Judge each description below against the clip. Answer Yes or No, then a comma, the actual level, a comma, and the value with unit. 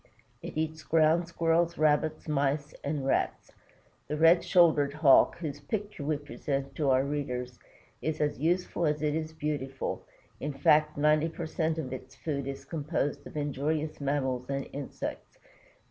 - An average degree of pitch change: No, narrow, 2.2 semitones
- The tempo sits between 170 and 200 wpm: No, average, 155 wpm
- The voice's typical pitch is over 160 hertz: No, medium, 150 Hz